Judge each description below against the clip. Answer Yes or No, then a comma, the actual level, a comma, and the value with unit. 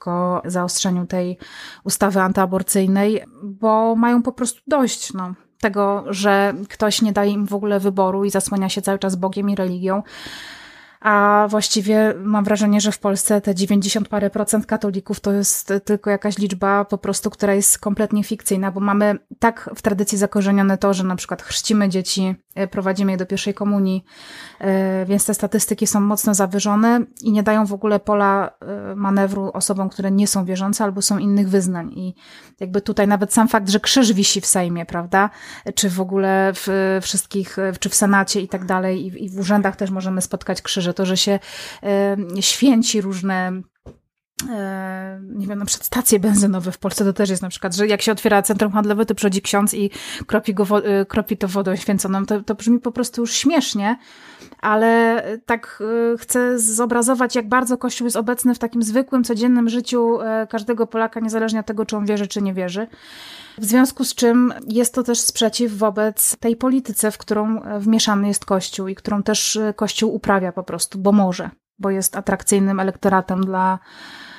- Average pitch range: No, narrow, 2.1 semitones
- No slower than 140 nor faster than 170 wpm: No, average, 180 wpm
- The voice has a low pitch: No, high, 205 Hz